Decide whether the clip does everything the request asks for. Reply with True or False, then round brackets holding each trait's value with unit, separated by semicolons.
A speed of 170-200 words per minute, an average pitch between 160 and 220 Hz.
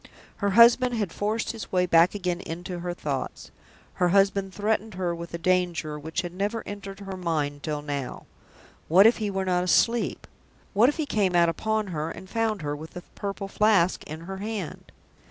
True (190 wpm; 185 Hz)